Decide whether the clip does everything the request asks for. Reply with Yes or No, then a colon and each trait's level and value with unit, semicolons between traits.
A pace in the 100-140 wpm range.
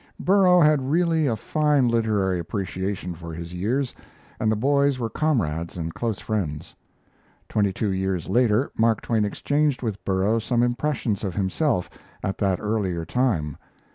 No: average, 150 wpm